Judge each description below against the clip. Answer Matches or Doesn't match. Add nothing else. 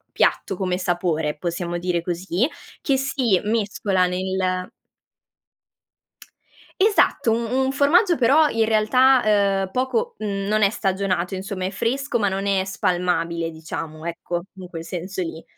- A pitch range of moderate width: Matches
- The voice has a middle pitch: Doesn't match